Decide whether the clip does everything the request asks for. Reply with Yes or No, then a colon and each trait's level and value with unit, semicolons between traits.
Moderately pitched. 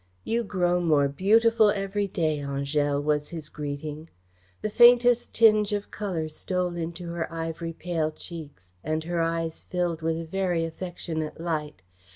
Yes: medium, 165 Hz